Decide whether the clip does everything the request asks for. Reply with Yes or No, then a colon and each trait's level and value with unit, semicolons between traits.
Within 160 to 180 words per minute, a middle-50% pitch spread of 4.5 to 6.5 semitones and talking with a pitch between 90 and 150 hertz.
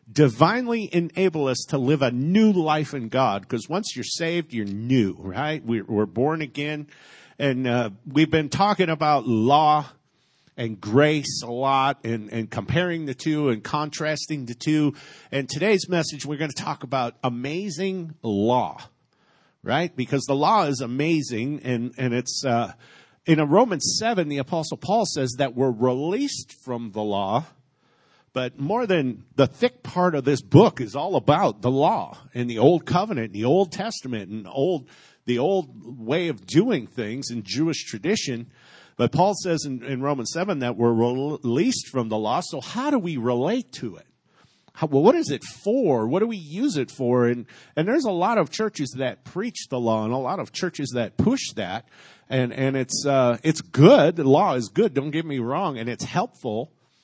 No: average, 190 wpm; average, 4.8 semitones; medium, 140 Hz